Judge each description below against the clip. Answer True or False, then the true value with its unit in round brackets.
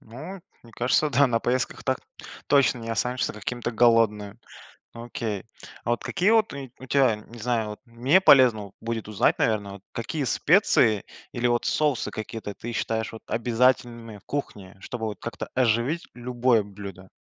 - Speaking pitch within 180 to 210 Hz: False (120 Hz)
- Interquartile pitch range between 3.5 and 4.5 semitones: False (2.8 semitones)